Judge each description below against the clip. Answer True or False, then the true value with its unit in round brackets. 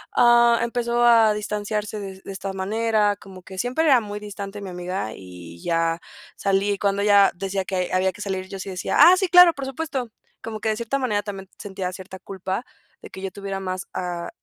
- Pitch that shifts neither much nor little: True (3.2 semitones)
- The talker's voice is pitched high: True (200 Hz)